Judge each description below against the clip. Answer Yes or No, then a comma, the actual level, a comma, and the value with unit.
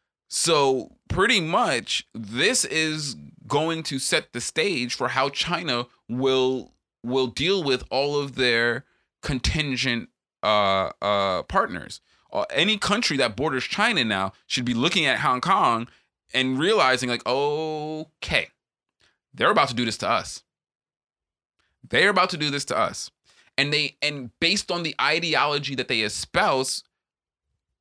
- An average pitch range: Yes, average, 3.6 semitones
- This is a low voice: Yes, low, 130 Hz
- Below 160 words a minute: Yes, average, 140 wpm